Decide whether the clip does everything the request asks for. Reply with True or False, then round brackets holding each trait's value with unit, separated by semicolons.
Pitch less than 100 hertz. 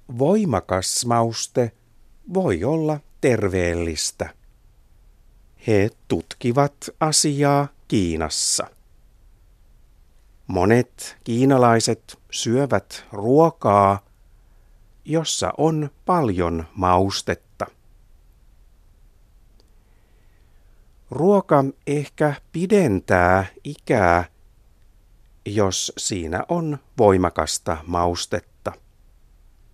False (110 Hz)